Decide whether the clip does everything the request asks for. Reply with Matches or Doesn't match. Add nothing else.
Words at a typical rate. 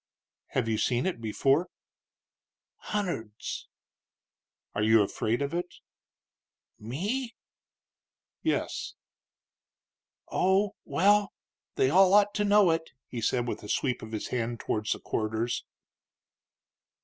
Doesn't match